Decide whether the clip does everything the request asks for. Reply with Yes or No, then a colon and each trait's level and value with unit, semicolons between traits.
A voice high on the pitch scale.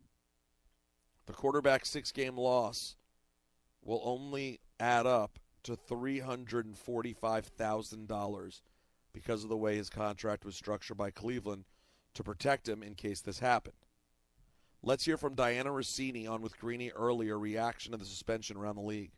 No: low, 110 Hz